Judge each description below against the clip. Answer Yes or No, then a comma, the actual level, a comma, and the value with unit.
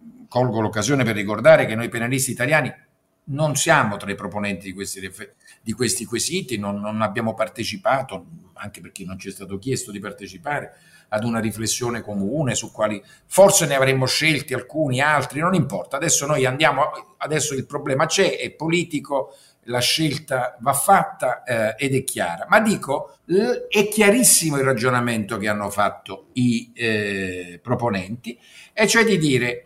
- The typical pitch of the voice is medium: No, low, 125 Hz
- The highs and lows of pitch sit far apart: Yes, wide, 6.2 semitones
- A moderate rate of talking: Yes, average, 160 wpm